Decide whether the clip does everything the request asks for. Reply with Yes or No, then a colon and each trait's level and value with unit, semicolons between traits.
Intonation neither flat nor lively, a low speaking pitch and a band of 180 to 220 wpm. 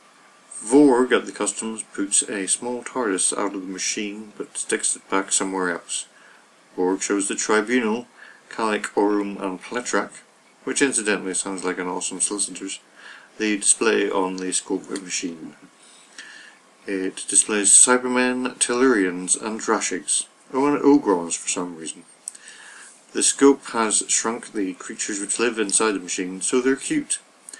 No: average, 4.5 semitones; low, 105 Hz; average, 145 wpm